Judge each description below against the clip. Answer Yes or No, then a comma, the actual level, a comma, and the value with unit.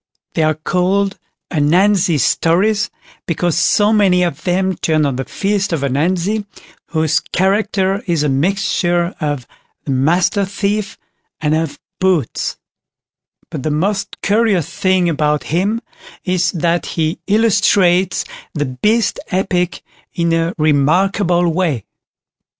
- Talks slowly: Yes, slow, 120 wpm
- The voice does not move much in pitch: No, average, 3.9 semitones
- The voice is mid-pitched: Yes, medium, 175 Hz